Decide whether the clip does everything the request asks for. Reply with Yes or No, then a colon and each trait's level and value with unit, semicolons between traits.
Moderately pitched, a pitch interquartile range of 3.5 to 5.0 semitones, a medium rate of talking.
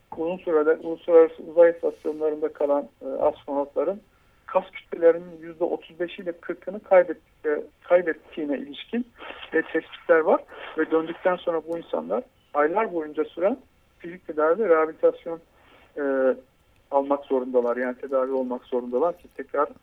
Yes: medium, 165 Hz; average, 4.3 semitones; average, 125 wpm